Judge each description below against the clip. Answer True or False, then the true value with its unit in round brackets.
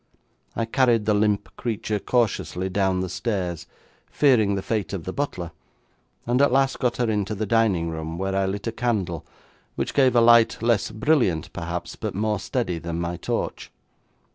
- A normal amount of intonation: True (4.4 semitones)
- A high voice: False (105 Hz)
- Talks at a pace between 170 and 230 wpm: True (175 wpm)